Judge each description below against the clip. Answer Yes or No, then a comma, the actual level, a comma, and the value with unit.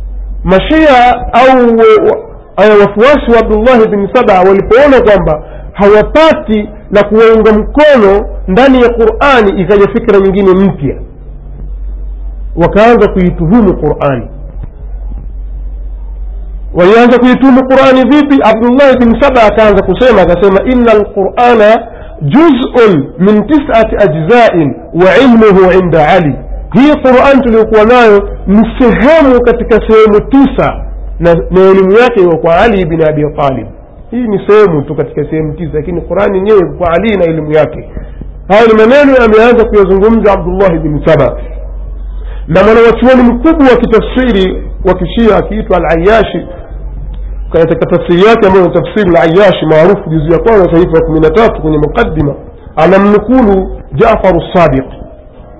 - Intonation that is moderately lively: No, wide, 6.3 semitones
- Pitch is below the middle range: No, high, 200 Hz